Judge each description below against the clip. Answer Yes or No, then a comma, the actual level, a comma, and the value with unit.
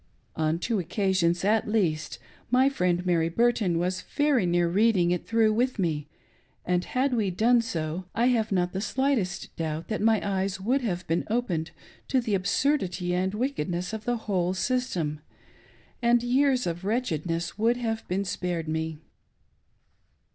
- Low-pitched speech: No, high, 190 Hz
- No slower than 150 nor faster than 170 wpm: Yes, average, 155 wpm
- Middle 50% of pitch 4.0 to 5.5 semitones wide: Yes, average, 5.1 semitones